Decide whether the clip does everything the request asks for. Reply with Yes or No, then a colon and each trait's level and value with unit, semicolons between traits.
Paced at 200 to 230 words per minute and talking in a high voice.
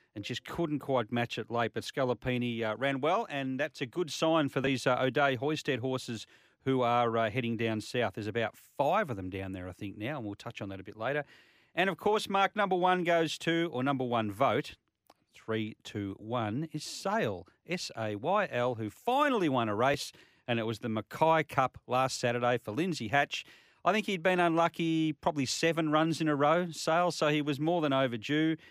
No: fast, 205 wpm; low, 135 Hz